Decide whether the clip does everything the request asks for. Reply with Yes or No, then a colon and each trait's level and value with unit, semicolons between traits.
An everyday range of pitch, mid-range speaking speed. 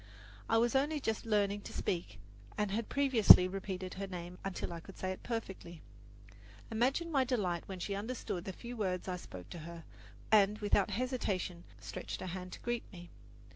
Yes: average, 4.1 semitones; average, 180 wpm